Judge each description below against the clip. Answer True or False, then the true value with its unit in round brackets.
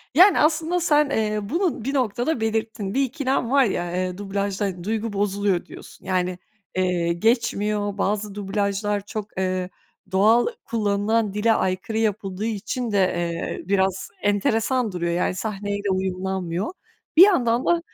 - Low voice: False (205 Hz)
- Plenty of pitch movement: False (3.2 semitones)